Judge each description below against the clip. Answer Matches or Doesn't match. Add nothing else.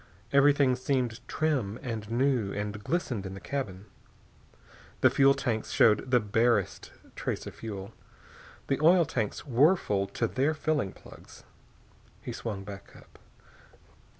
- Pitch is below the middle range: Matches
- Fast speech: Doesn't match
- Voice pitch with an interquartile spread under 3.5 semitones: Doesn't match